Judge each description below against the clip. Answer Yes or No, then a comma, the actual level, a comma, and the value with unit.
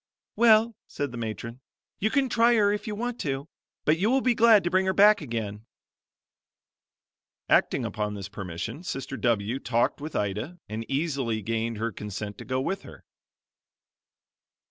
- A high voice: No, low, 135 Hz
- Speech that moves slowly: No, average, 165 wpm